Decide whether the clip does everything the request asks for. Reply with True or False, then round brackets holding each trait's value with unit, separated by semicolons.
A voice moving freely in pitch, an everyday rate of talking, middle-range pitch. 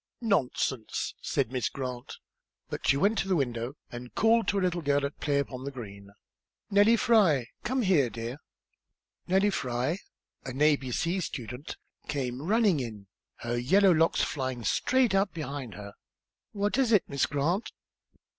True (7.6 semitones; 160 wpm; 145 Hz)